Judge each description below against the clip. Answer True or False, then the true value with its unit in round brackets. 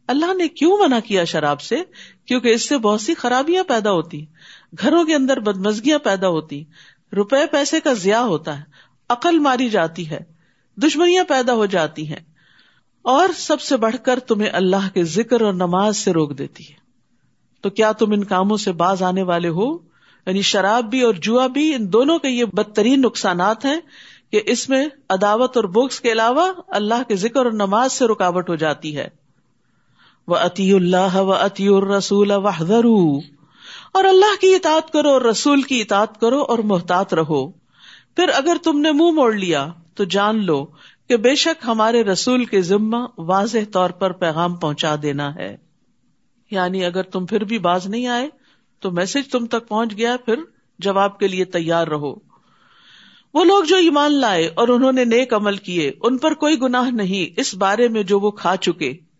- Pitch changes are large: True (5.7 semitones)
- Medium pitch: False (215 Hz)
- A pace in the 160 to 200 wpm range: True (180 wpm)